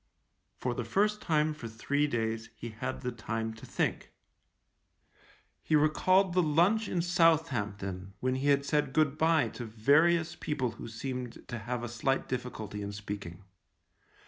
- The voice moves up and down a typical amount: No, wide, 5.8 semitones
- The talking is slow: No, average, 155 wpm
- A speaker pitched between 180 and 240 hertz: No, low, 130 Hz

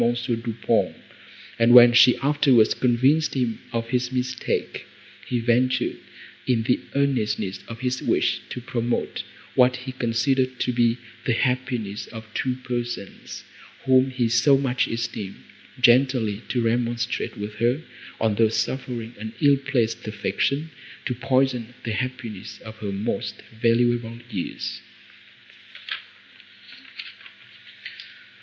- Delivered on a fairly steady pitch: Yes, narrow, 2.1 semitones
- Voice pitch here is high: No, low, 120 Hz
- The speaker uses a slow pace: Yes, slow, 120 wpm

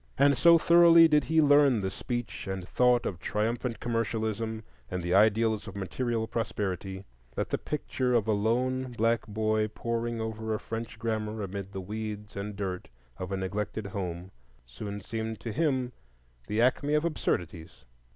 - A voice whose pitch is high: No, low, 110 Hz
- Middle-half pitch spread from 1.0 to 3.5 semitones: Yes, average, 3.2 semitones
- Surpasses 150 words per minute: Yes, average, 160 wpm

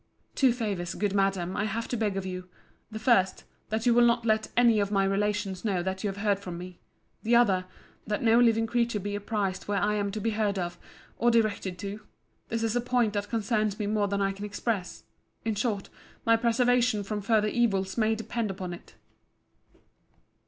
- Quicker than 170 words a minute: Yes, average, 190 wpm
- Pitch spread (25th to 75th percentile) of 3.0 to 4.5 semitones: No, narrow, 2.6 semitones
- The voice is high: Yes, high, 210 Hz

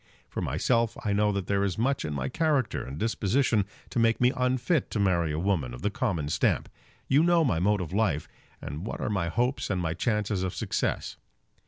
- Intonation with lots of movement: Yes, wide, 5.7 semitones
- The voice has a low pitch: Yes, low, 100 Hz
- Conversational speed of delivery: No, fast, 210 wpm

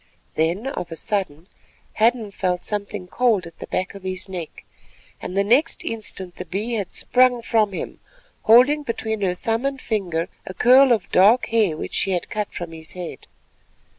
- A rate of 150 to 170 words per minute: No, average, 180 wpm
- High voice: Yes, high, 205 Hz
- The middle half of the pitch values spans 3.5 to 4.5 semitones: Yes, average, 4.2 semitones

